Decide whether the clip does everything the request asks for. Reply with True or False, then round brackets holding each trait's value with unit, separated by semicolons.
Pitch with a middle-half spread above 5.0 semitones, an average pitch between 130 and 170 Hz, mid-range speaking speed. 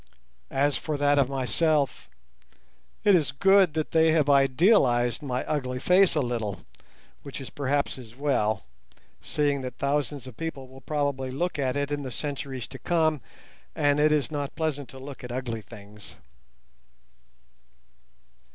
False (2.7 semitones; 140 Hz; 150 wpm)